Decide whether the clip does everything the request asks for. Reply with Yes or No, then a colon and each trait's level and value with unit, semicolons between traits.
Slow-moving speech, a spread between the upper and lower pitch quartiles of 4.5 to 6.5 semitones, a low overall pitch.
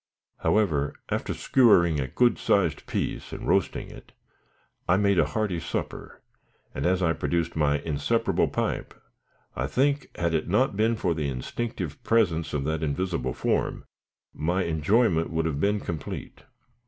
No: average, 150 wpm; average, 5.2 semitones; very low, 85 Hz